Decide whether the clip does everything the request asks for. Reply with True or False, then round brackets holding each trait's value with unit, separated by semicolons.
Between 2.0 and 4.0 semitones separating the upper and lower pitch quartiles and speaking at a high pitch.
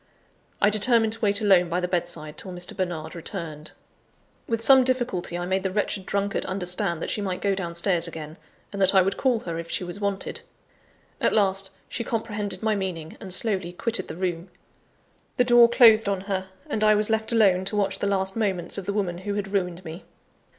True (3.1 semitones; 195 Hz)